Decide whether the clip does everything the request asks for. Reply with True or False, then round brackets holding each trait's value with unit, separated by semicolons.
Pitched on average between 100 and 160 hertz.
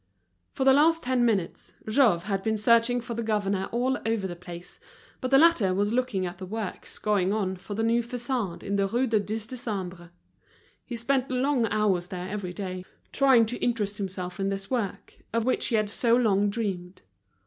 False (215 Hz)